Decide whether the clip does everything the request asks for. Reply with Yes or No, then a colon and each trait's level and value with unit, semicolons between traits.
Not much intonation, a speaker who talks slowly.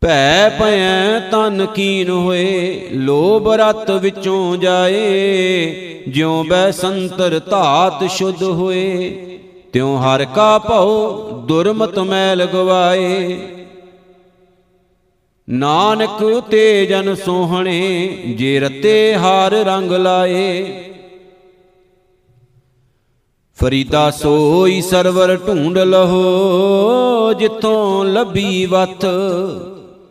Yes: narrow, 1.3 semitones; slow, 75 wpm